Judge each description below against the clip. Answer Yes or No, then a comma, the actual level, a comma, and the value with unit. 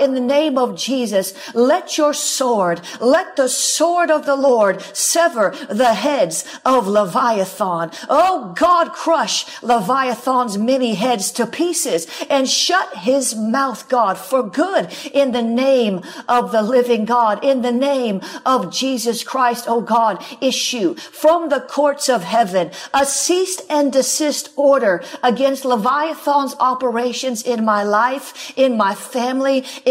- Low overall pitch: No, very high, 260 Hz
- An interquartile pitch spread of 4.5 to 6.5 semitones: No, average, 3.6 semitones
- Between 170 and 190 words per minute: No, average, 140 wpm